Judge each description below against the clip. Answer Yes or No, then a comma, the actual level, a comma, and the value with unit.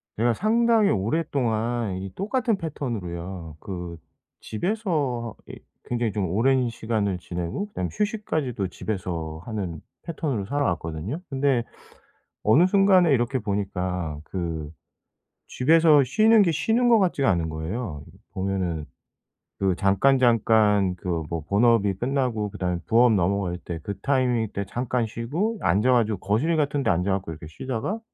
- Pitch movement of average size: No, wide, 7.1 semitones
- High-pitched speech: No, low, 110 Hz